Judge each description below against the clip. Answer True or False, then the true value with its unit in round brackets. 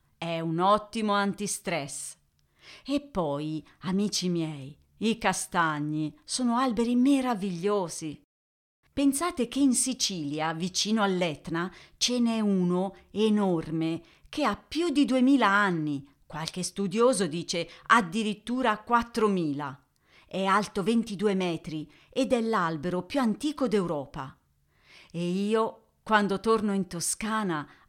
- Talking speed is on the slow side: True (110 wpm)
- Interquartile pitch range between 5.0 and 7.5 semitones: True (5.3 semitones)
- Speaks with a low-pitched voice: False (195 Hz)